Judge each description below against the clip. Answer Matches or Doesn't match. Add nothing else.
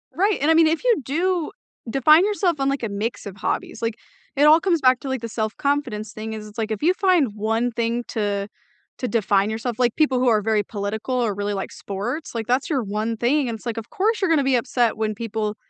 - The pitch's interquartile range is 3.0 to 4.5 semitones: Doesn't match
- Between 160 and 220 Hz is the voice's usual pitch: Doesn't match